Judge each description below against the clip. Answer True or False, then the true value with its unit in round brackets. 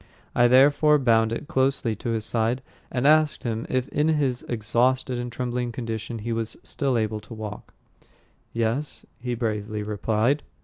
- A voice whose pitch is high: False (120 Hz)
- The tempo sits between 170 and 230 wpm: False (160 wpm)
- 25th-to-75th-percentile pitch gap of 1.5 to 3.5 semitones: True (2.8 semitones)